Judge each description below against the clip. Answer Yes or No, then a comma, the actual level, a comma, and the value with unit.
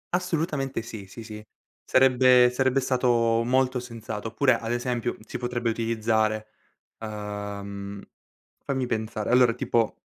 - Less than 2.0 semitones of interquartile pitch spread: No, average, 2.7 semitones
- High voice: No, low, 115 Hz